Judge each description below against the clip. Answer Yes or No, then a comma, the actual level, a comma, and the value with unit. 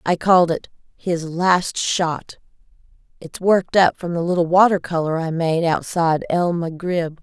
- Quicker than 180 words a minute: No, average, 160 wpm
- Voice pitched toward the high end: No, medium, 170 Hz